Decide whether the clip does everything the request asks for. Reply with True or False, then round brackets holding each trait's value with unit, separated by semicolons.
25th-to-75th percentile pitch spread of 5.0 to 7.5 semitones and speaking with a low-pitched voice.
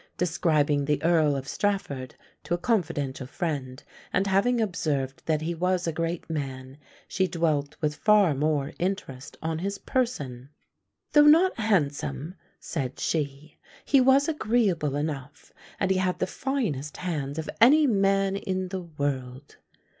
False (5.5 semitones; 165 Hz)